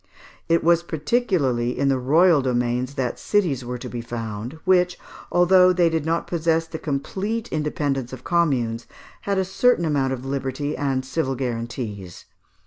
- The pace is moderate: Yes, average, 155 wpm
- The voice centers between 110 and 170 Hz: Yes, medium, 140 Hz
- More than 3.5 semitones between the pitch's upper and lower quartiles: Yes, wide, 5.4 semitones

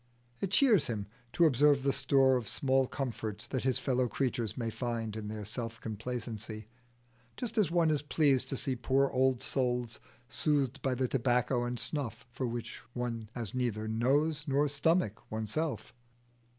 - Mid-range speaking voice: No, low, 125 Hz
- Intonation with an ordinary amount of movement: Yes, average, 3.2 semitones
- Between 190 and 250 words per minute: No, average, 165 wpm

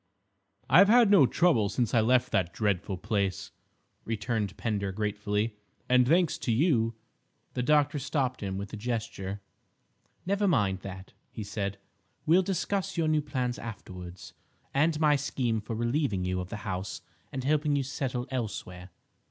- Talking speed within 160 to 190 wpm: No, average, 150 wpm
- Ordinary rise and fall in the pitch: No, wide, 6.3 semitones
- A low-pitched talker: Yes, low, 115 Hz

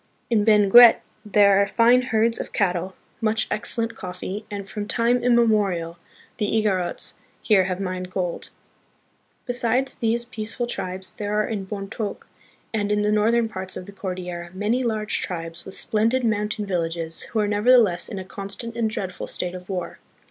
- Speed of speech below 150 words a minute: No, average, 165 wpm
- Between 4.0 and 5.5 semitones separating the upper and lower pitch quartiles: No, average, 3.2 semitones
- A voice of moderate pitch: No, high, 210 Hz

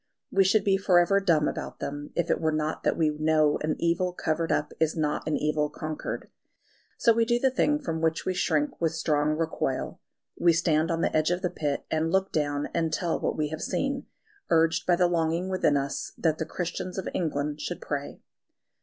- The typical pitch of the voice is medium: Yes, medium, 160 Hz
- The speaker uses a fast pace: Yes, fast, 210 wpm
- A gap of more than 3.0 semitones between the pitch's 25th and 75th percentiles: No, narrow, 2.6 semitones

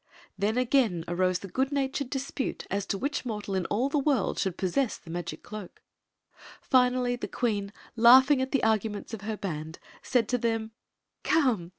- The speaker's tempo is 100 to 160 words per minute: No, average, 180 wpm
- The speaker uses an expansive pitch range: No, average, 4.9 semitones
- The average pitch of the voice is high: Yes, high, 225 Hz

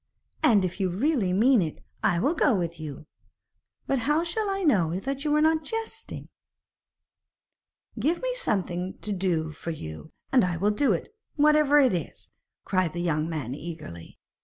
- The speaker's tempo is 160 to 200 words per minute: Yes, average, 170 wpm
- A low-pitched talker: No, high, 195 Hz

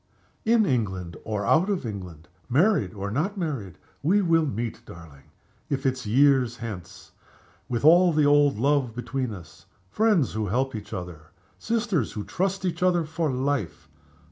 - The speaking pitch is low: Yes, low, 130 Hz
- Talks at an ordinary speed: Yes, average, 155 wpm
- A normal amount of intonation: No, wide, 8.0 semitones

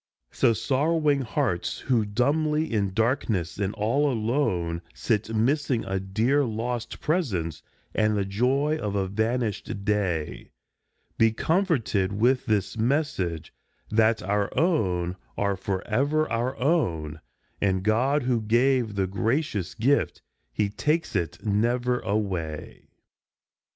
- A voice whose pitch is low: Yes, low, 110 Hz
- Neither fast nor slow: No, slow, 120 wpm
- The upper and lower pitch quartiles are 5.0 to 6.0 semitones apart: Yes, average, 5.3 semitones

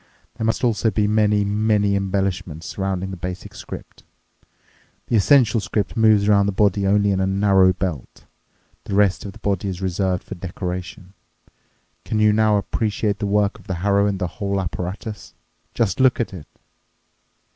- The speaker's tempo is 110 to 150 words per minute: No, average, 165 wpm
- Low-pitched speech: Yes, low, 100 Hz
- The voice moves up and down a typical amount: No, narrow, 1.9 semitones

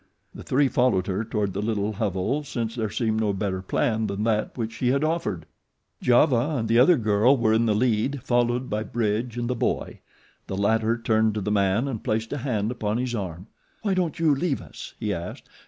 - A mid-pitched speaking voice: No, low, 110 Hz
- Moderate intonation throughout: Yes, average, 3.1 semitones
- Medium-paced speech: No, fast, 210 wpm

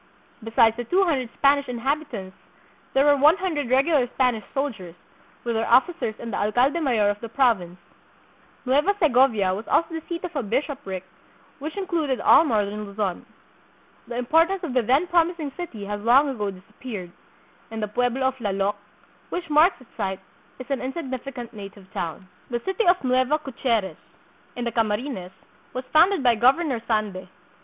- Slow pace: No, average, 165 wpm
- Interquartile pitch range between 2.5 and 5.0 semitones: No, wide, 5.6 semitones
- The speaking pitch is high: Yes, very high, 250 Hz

